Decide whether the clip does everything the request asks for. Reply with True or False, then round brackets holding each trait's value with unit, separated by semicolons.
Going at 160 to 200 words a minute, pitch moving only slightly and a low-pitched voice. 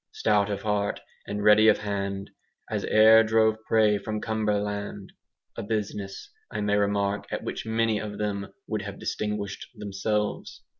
False (150 wpm; 1.2 semitones; 105 Hz)